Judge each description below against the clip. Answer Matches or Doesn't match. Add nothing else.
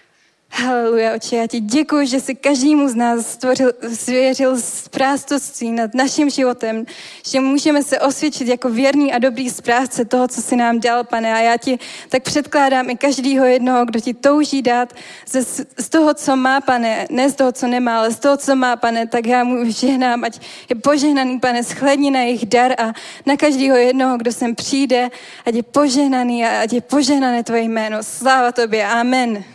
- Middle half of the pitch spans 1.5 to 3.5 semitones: Matches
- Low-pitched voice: Doesn't match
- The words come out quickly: Matches